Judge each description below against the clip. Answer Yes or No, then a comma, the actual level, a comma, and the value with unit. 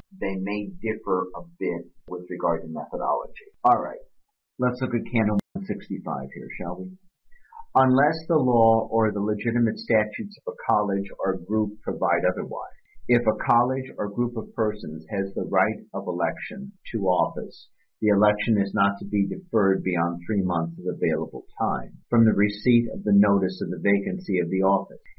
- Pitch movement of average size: Yes, average, 3.7 semitones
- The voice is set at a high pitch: No, low, 105 Hz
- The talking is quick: No, average, 170 wpm